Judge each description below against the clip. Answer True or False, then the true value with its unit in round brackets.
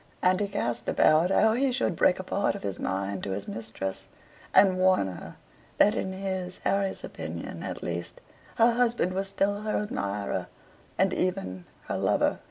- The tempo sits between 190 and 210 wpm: False (175 wpm)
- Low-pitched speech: False (185 Hz)